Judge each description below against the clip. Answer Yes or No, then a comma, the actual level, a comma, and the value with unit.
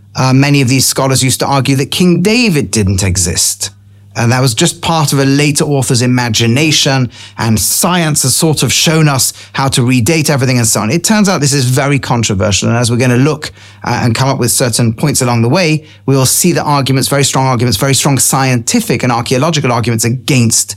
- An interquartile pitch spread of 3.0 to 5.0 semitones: Yes, average, 3.8 semitones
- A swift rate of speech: Yes, fast, 215 wpm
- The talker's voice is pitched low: Yes, low, 130 Hz